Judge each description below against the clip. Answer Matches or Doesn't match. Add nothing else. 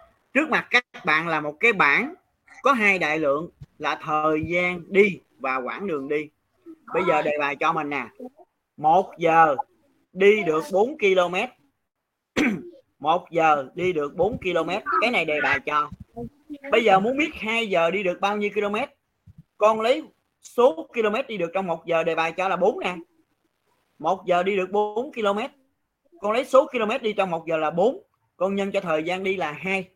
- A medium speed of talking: Matches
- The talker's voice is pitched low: Doesn't match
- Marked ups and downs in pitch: Matches